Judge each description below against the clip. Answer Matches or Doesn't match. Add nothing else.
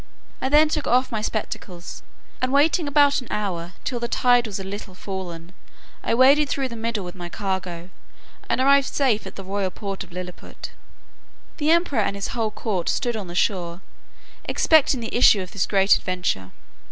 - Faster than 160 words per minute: Matches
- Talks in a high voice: Matches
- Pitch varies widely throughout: Matches